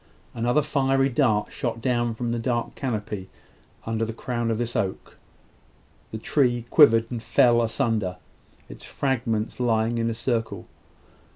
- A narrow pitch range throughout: Yes, narrow, 1.7 semitones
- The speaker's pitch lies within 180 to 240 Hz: No, low, 115 Hz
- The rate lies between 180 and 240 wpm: No, average, 145 wpm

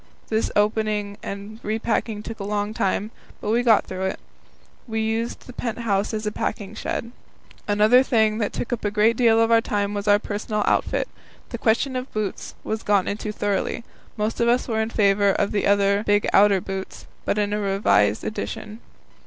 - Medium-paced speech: Yes, average, 190 wpm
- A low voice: No, high, 210 Hz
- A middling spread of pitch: No, narrow, 1.7 semitones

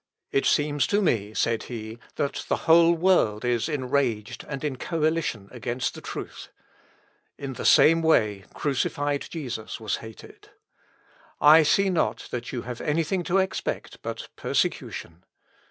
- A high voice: No, low, 135 Hz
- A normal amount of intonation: No, wide, 5.7 semitones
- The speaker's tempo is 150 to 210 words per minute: No, average, 140 wpm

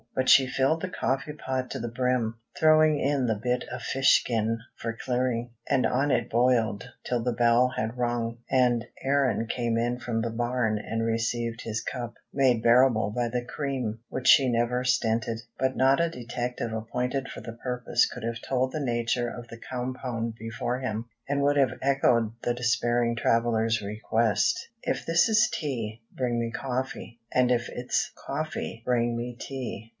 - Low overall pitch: Yes, low, 120 Hz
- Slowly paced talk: No, average, 175 wpm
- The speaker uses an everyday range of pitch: No, narrow, 2.1 semitones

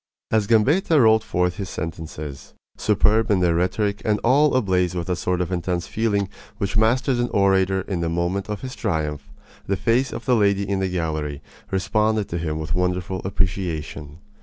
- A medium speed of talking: Yes, average, 180 wpm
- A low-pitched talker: Yes, very low, 95 Hz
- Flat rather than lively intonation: No, average, 3.7 semitones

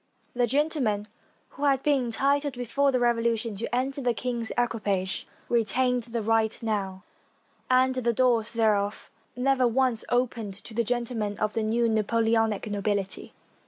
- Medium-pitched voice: No, high, 235 Hz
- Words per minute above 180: No, average, 145 wpm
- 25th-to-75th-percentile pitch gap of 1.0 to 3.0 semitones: Yes, average, 2.7 semitones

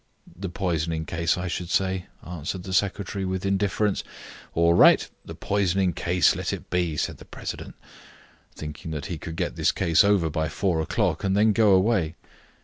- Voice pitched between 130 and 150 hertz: No, very low, 90 Hz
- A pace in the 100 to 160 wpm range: No, average, 175 wpm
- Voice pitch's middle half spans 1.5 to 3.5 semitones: Yes, average, 2.9 semitones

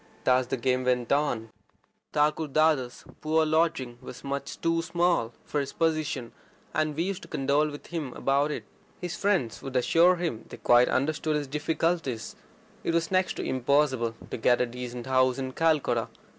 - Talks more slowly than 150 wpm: No, average, 170 wpm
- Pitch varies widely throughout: No, average, 4.1 semitones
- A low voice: No, medium, 145 Hz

